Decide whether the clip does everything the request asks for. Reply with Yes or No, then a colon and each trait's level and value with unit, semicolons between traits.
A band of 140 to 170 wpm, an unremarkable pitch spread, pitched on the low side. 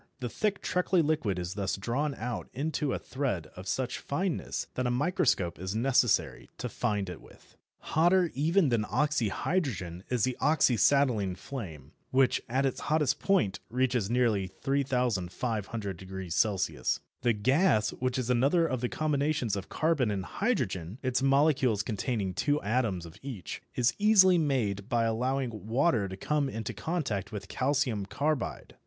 No: average, 150 wpm; wide, 5.9 semitones; low, 125 Hz